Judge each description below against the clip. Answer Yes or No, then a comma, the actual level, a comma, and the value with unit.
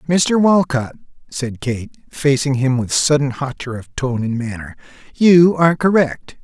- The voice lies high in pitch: No, medium, 140 Hz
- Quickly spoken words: No, average, 150 wpm